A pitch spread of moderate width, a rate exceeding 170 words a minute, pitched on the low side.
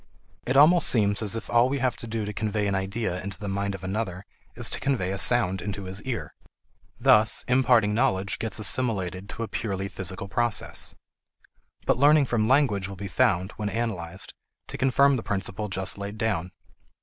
Yes: average, 3.6 semitones; average, 185 wpm; low, 105 Hz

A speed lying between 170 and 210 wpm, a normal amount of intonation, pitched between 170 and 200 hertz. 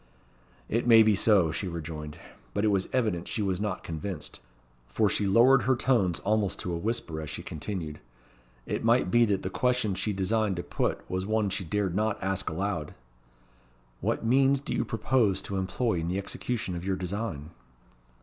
No: average, 185 wpm; average, 3.8 semitones; low, 100 Hz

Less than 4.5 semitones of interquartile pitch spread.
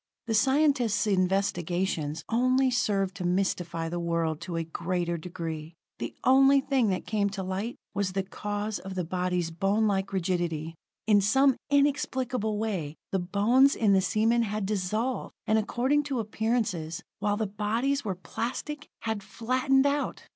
No: average, 4.9 semitones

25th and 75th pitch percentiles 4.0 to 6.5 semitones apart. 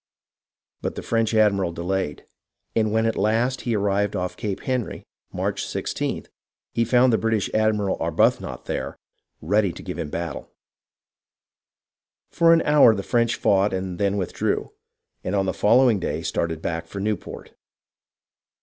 No: average, 3.1 semitones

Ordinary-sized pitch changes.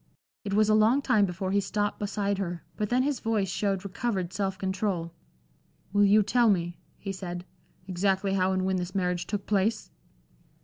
No: narrow, 2.1 semitones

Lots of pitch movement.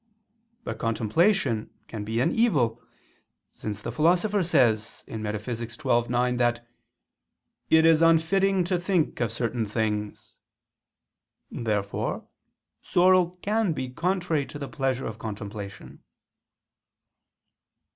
Yes: wide, 7.5 semitones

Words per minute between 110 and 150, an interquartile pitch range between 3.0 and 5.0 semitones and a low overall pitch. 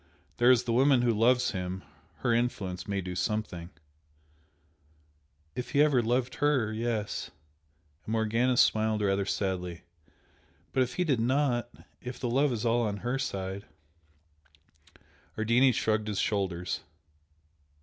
Yes: average, 140 wpm; average, 4.1 semitones; low, 115 Hz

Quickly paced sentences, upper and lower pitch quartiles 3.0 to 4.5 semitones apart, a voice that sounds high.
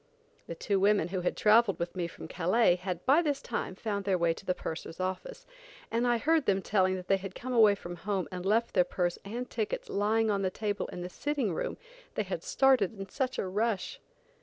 Yes: fast, 225 wpm; average, 3.9 semitones; high, 200 Hz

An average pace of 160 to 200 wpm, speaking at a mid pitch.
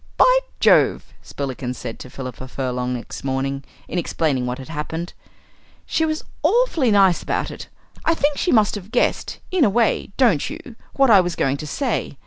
Yes: average, 180 wpm; medium, 175 Hz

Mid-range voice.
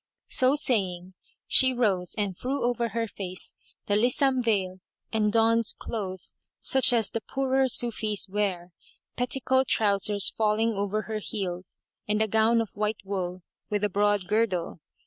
No: high, 215 Hz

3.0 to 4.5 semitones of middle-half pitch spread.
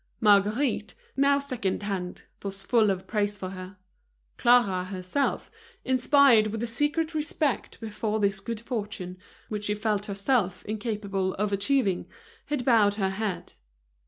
Yes: average, 3.7 semitones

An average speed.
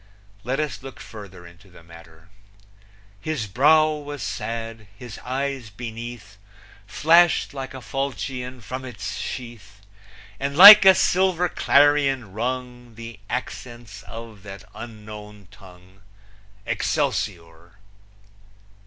No: slow, 110 wpm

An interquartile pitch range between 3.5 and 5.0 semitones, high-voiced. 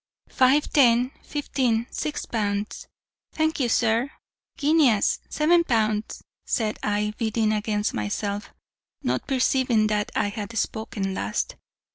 Yes: average, 3.8 semitones; high, 225 Hz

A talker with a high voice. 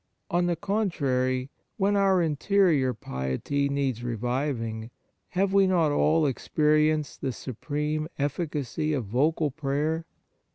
No: medium, 150 Hz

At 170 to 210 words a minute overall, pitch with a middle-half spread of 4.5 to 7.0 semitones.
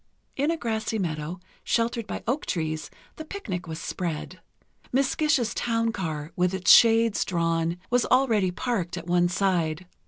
No: average, 155 wpm; wide, 5.6 semitones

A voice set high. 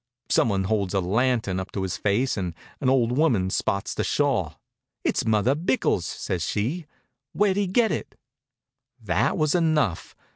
No: low, 115 Hz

